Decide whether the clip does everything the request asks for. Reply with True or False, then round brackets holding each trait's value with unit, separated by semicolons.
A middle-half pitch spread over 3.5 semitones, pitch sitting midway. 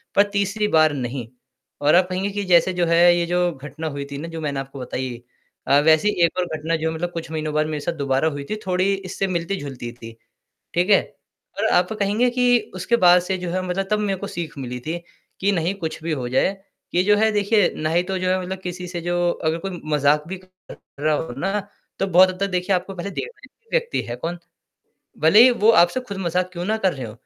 True (3.9 semitones; 175 Hz)